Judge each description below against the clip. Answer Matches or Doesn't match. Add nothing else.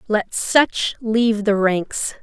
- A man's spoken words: Doesn't match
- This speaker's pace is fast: Doesn't match